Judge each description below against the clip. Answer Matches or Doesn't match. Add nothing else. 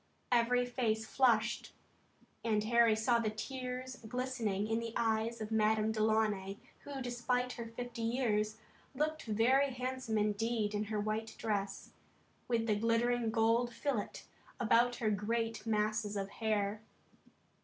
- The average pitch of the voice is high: Matches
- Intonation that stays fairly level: Matches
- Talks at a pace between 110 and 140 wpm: Matches